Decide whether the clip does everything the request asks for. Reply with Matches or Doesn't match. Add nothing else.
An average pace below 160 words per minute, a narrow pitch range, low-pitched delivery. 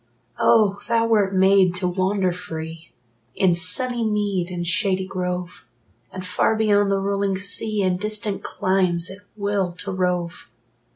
Doesn't match